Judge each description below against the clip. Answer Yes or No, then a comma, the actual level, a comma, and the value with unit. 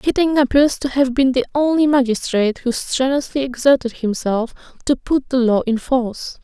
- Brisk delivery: No, average, 170 wpm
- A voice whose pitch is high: Yes, very high, 260 Hz